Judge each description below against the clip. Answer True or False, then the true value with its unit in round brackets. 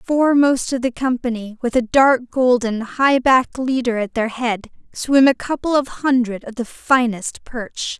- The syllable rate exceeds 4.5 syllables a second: False (4.3 syllables/s)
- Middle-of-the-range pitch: False (250 Hz)